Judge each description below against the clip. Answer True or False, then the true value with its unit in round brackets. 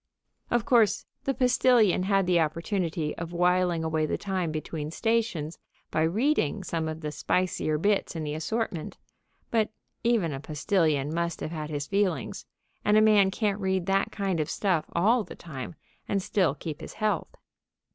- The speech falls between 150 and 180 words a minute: True (170 wpm)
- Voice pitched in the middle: True (180 Hz)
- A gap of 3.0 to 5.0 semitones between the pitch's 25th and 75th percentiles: True (4.7 semitones)